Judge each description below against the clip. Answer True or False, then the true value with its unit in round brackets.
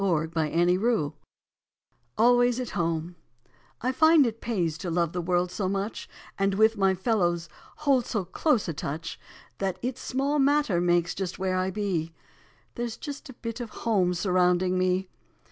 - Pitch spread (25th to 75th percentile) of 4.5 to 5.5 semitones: True (5.2 semitones)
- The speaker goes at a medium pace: True (160 wpm)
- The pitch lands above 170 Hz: True (190 Hz)